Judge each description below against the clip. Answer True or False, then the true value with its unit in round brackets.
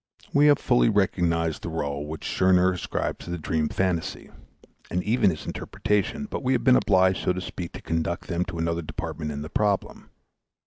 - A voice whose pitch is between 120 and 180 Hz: False (90 Hz)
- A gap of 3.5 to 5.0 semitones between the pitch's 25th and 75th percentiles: True (3.9 semitones)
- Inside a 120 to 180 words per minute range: False (190 wpm)